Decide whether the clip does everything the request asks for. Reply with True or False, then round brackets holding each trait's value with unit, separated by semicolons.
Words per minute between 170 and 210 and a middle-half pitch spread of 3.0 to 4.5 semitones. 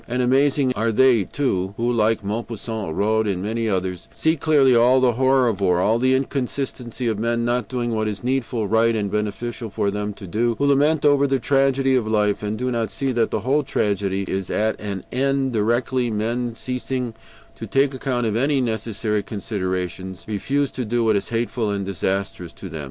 True (195 wpm; 3.7 semitones)